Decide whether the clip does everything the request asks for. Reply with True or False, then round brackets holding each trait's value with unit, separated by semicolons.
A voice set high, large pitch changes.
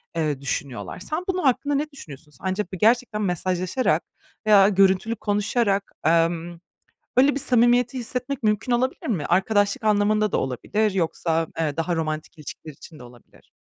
True (200 Hz; 6.4 semitones)